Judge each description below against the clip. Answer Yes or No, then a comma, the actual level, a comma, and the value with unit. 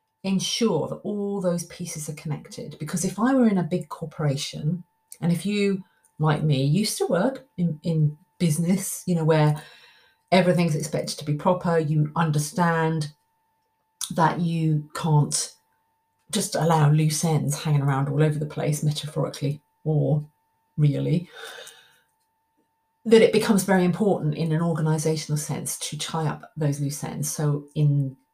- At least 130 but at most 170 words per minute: Yes, average, 145 wpm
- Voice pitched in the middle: Yes, medium, 165 Hz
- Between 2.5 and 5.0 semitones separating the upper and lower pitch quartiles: Yes, average, 4.5 semitones